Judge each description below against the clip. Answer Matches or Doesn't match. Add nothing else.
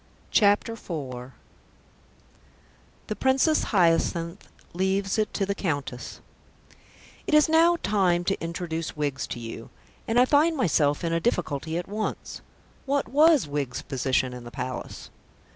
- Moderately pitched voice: Matches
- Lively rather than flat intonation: Matches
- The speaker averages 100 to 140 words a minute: Matches